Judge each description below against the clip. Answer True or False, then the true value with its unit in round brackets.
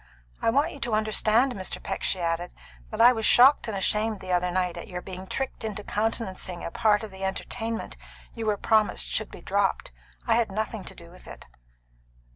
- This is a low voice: False (215 Hz)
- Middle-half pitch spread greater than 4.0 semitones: False (3.3 semitones)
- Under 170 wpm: False (205 wpm)